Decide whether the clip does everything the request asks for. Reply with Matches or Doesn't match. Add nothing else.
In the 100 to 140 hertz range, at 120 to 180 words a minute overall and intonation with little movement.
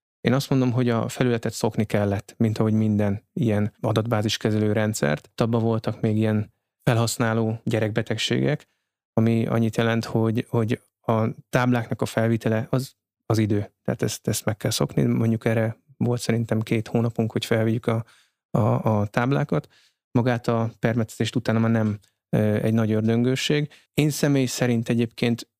Matches